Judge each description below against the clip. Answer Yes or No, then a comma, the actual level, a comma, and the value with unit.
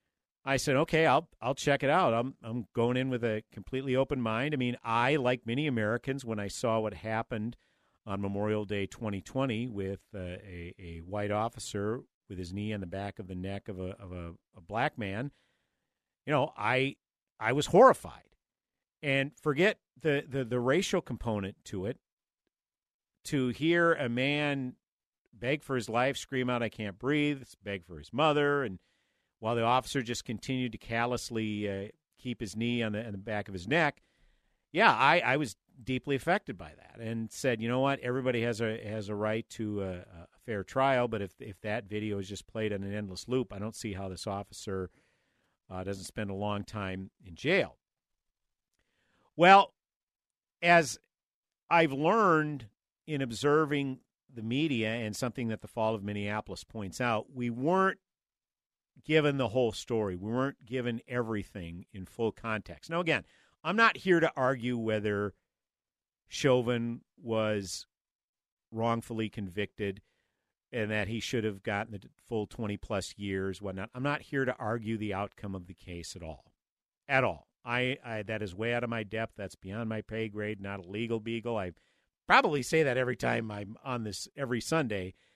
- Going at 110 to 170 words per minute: No, average, 180 wpm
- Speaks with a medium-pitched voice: No, low, 115 Hz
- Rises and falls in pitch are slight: No, average, 4.1 semitones